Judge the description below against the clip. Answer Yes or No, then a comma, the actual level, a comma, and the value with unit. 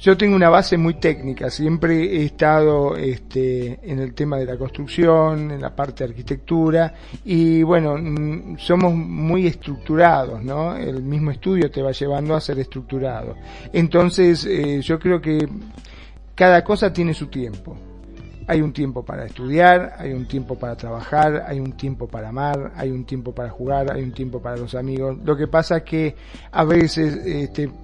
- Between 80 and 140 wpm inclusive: No, average, 175 wpm